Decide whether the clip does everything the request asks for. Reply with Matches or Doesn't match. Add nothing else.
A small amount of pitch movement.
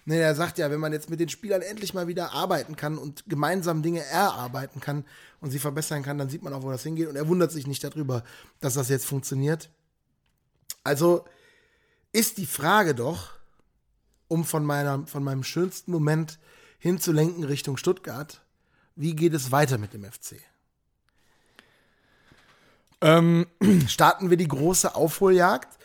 Doesn't match